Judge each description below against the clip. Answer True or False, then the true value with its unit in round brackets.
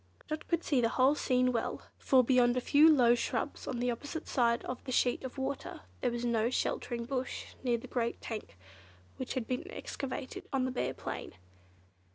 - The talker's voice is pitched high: True (255 Hz)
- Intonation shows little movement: True (2.1 semitones)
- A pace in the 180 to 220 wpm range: True (195 wpm)